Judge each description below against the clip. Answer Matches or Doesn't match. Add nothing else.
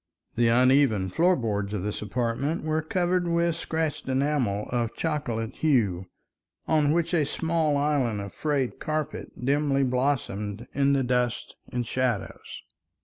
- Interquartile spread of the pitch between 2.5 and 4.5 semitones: Doesn't match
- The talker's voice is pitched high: Doesn't match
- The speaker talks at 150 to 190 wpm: Doesn't match